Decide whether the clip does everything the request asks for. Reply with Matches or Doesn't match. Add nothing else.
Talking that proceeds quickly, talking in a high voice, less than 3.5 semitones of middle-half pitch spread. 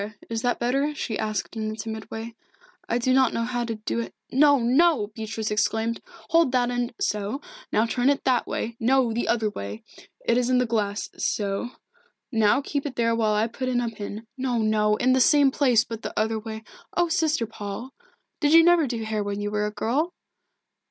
Matches